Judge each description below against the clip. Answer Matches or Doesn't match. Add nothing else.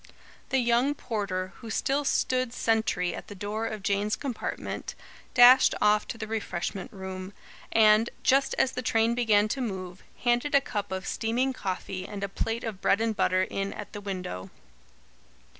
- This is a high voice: Matches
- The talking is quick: Doesn't match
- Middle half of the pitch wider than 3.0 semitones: Matches